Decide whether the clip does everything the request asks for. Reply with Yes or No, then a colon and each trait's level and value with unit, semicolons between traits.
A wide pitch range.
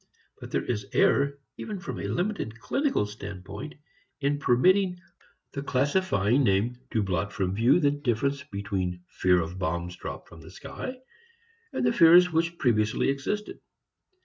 Yes: wide, 8.2 semitones